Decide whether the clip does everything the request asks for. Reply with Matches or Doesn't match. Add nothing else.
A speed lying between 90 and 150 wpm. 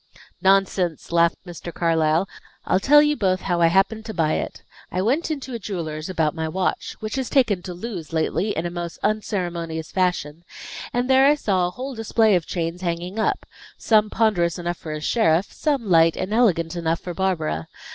Doesn't match